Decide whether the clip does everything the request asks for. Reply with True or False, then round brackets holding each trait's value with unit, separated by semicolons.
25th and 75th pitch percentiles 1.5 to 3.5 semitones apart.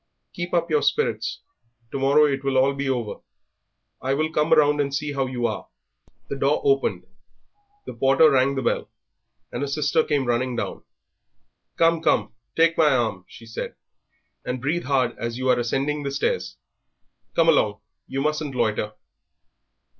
True (2.8 semitones)